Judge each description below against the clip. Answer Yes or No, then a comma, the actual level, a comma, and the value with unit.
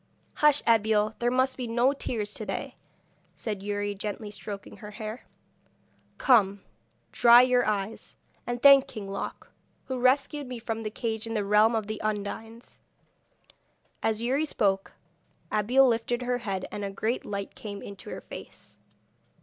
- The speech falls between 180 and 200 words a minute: No, average, 155 wpm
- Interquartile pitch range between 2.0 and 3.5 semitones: Yes, average, 3.0 semitones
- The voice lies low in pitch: No, high, 220 Hz